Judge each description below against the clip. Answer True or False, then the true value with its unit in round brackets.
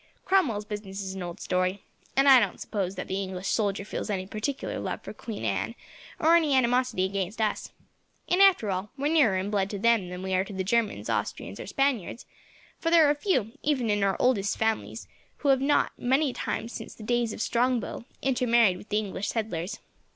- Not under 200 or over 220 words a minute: True (205 wpm)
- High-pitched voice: True (215 Hz)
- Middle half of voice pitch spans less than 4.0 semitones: False (5.0 semitones)